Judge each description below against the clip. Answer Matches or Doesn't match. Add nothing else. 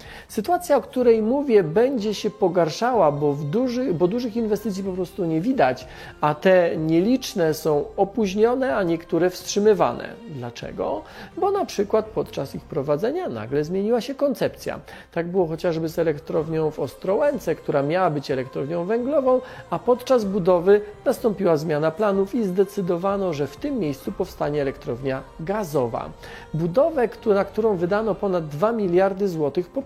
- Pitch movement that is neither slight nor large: Doesn't match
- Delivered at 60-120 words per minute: Doesn't match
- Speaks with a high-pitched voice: Matches